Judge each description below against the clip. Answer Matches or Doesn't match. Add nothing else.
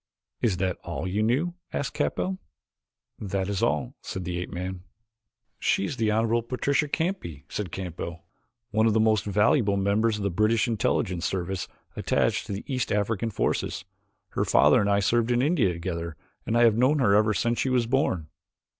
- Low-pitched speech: Matches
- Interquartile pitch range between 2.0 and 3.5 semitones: Doesn't match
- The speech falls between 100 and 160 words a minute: Doesn't match